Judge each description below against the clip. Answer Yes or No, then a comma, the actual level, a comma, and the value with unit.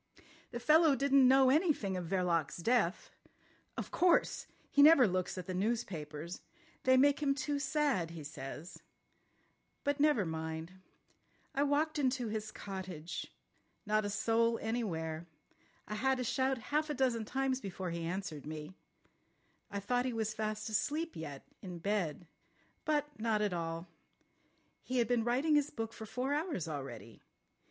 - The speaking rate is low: No, average, 150 wpm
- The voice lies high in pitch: Yes, high, 220 Hz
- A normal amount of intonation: No, wide, 7.5 semitones